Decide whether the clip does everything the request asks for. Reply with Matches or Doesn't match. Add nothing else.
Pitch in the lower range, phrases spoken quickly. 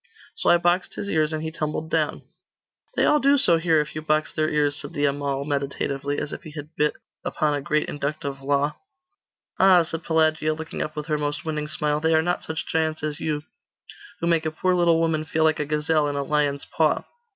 Doesn't match